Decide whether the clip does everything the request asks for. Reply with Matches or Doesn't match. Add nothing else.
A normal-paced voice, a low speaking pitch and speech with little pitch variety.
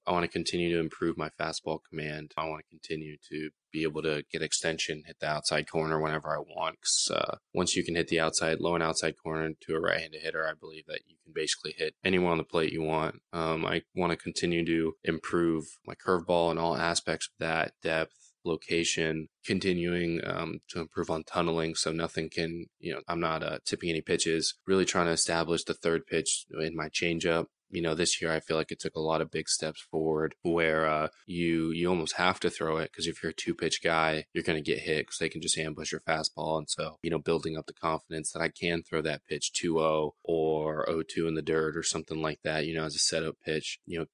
Doesn't match